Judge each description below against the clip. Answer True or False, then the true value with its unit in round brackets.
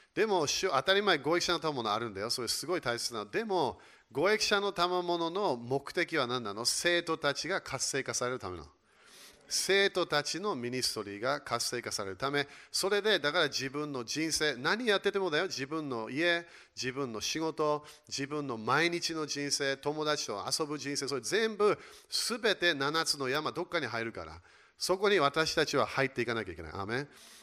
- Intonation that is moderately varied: True (4.6 semitones)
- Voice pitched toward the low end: False (150 Hz)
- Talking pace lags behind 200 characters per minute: False (355 characters per minute)